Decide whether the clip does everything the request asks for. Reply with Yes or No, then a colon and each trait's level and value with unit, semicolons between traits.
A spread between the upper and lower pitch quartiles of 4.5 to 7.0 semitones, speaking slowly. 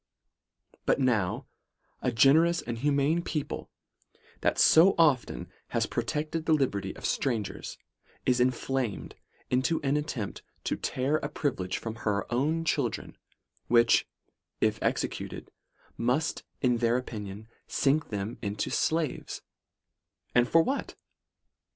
Yes: average, 4.8 semitones; slow, 115 wpm